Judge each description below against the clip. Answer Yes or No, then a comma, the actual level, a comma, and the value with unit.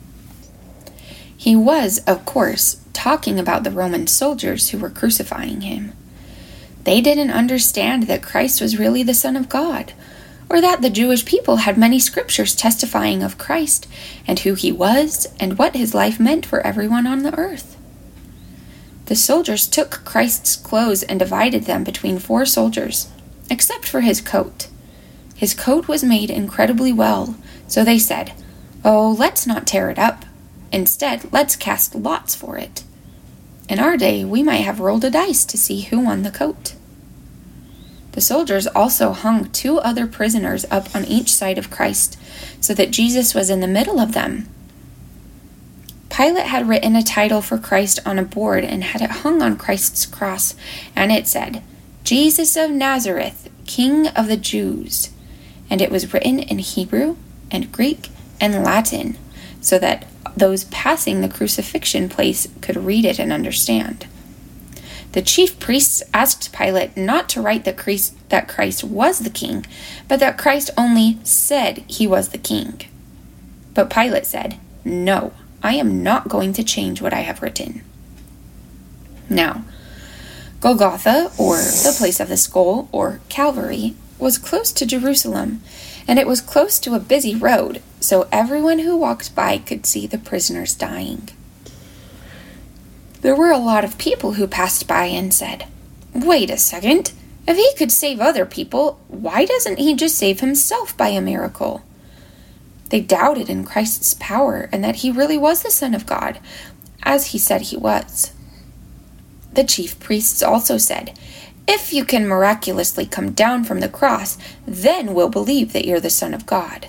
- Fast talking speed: No, average, 160 wpm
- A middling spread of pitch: No, wide, 6.2 semitones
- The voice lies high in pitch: Yes, high, 235 Hz